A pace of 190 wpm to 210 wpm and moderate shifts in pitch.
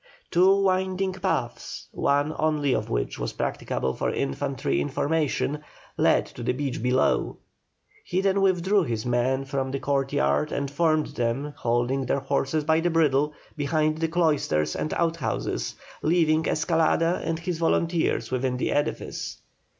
No: average, 145 wpm; average, 4.0 semitones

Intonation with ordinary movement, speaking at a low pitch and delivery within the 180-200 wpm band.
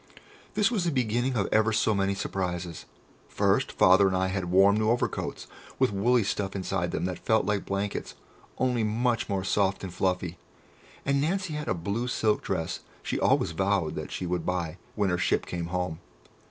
Yes: average, 3.8 semitones; low, 100 Hz; average, 185 wpm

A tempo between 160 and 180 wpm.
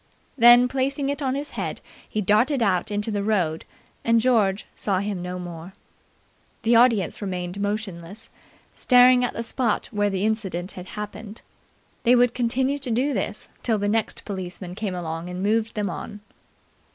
Yes: average, 165 wpm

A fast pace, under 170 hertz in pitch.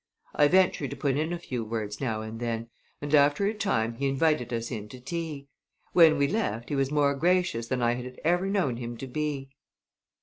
Yes: fast, 210 wpm; medium, 140 Hz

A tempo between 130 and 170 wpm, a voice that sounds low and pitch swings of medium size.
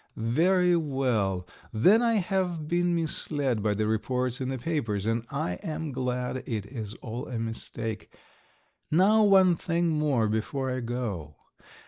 No: average, 145 wpm; low, 130 Hz; wide, 6.8 semitones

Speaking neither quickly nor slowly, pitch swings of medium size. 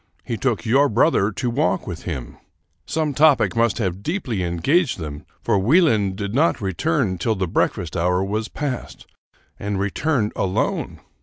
No: average, 155 wpm; wide, 6.8 semitones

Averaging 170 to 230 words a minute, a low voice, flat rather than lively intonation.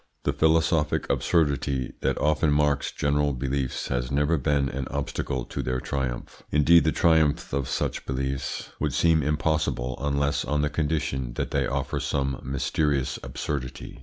No: average, 150 wpm; very low, 70 Hz; narrow, 2.1 semitones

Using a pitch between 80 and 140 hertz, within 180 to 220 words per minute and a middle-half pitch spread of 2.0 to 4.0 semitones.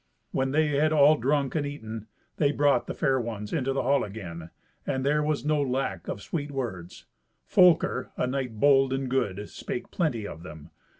No: low, 135 Hz; average, 185 wpm; average, 4.7 semitones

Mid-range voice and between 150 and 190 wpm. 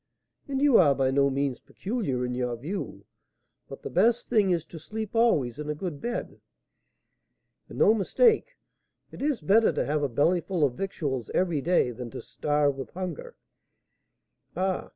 Yes: medium, 165 Hz; average, 170 wpm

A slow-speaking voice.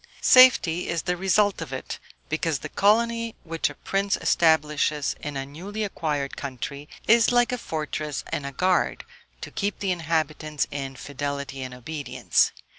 No: average, 155 wpm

